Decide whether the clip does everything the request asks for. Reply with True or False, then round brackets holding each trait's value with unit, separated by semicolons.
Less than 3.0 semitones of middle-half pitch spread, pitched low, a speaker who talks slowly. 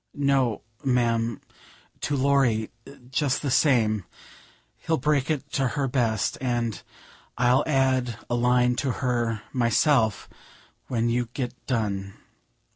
True (2.6 semitones; 125 Hz; 120 wpm)